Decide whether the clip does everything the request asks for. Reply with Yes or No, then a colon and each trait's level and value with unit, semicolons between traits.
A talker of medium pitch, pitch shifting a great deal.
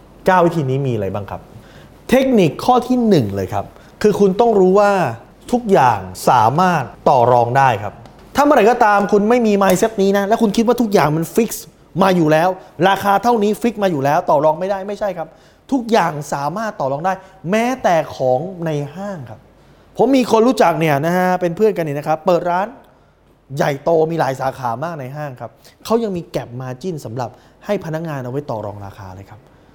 Yes: medium, 170 Hz; wide, 7.1 semitones